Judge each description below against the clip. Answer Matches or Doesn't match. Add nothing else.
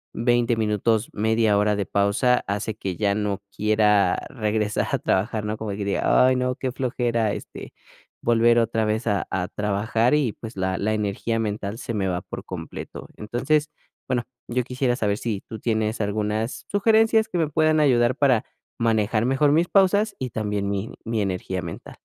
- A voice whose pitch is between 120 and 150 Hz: Doesn't match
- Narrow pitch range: Doesn't match